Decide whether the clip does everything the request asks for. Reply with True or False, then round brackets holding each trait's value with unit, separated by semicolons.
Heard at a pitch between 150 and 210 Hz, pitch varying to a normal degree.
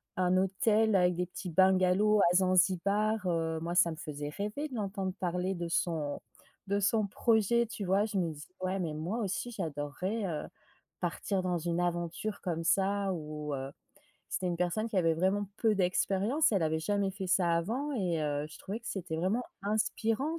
True (185 Hz; 3.3 semitones)